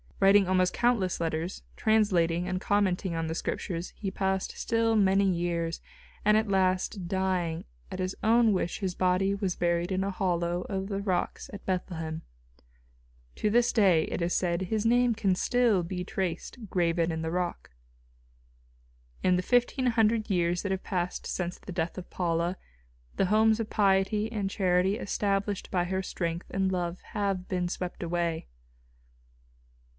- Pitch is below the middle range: No, medium, 185 Hz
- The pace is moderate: Yes, average, 160 wpm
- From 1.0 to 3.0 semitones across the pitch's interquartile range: Yes, narrow, 2.6 semitones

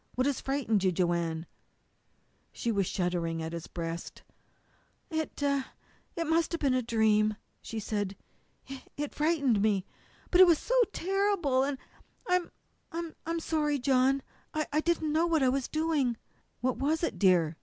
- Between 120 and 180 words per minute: Yes, average, 155 wpm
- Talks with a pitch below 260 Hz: No, very high, 270 Hz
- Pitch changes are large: Yes, wide, 7.5 semitones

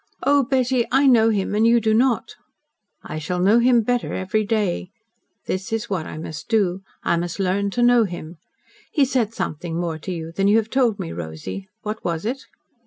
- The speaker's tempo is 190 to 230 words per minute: Yes, average, 200 wpm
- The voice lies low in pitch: No, high, 205 Hz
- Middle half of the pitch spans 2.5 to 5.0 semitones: No, wide, 5.4 semitones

